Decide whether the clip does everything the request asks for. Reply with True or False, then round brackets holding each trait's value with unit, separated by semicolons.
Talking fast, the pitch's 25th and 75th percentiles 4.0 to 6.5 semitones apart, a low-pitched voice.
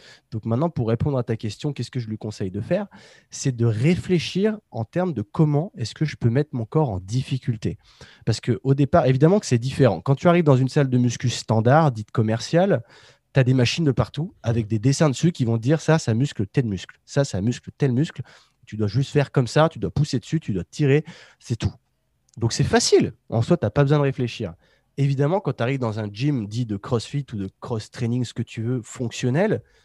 True (230 wpm; 4.3 semitones; 130 Hz)